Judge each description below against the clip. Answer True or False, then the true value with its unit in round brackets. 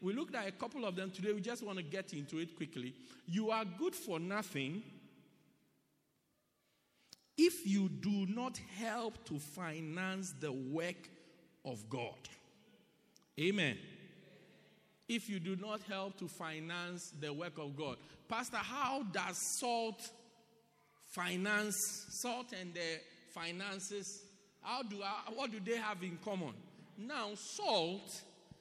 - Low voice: False (195 Hz)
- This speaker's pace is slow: True (130 wpm)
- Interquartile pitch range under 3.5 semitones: False (3.9 semitones)